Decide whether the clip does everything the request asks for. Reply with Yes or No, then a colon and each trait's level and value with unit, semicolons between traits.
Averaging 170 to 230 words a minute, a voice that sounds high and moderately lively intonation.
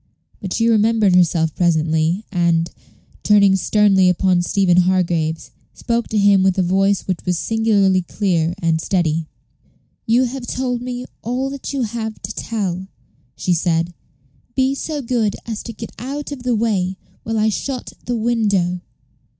No: average, 155 wpm; high, 200 Hz; average, 4.6 semitones